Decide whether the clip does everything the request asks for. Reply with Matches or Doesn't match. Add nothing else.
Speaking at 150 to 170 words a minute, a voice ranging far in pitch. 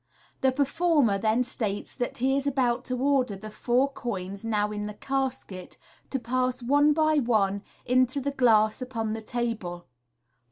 Doesn't match